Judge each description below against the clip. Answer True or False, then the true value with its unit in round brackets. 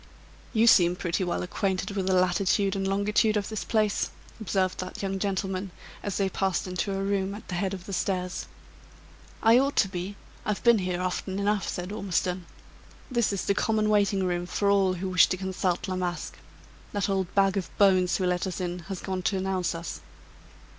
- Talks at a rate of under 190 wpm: False (195 wpm)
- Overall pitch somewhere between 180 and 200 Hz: True (190 Hz)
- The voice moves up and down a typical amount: False (1.7 semitones)